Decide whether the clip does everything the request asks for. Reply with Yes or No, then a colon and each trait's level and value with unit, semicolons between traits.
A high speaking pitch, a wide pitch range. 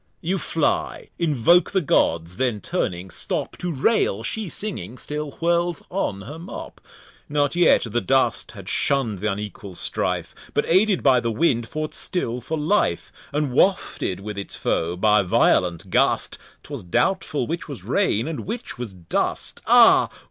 No: low, 130 Hz; wide, 8.8 semitones